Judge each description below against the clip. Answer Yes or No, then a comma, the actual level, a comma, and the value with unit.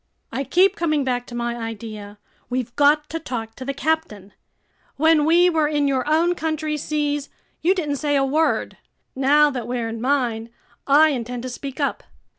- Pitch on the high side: Yes, very high, 280 Hz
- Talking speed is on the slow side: No, average, 180 wpm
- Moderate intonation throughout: Yes, average, 4.0 semitones